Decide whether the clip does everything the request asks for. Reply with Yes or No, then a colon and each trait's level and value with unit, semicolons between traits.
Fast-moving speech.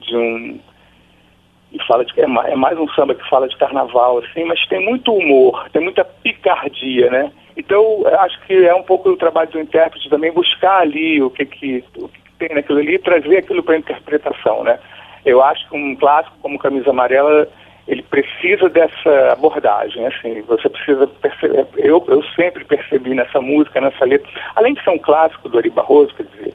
Yes: fast, 190 wpm